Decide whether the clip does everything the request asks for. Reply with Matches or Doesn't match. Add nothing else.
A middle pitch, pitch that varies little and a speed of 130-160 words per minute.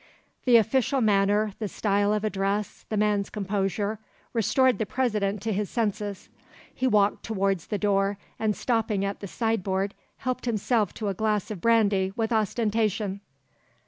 Doesn't match